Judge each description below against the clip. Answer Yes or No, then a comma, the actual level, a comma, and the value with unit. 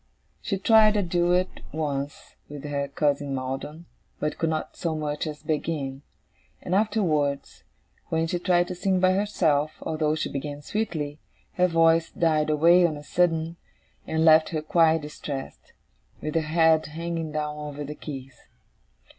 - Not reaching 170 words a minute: Yes, average, 155 wpm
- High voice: No, medium, 155 Hz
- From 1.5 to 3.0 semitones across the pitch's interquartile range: Yes, narrow, 2.6 semitones